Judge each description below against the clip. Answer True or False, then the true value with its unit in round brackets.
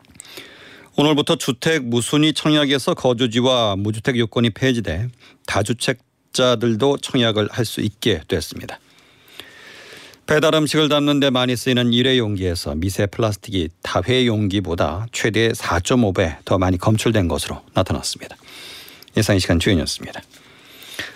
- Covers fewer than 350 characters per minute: True (300 characters per minute)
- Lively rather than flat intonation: False (4.3 semitones)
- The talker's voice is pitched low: True (120 Hz)